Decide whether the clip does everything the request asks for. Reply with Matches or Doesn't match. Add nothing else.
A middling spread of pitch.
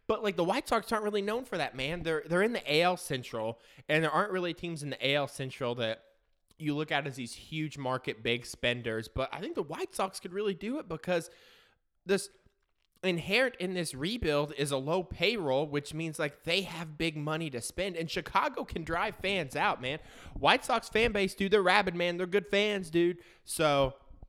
Doesn't match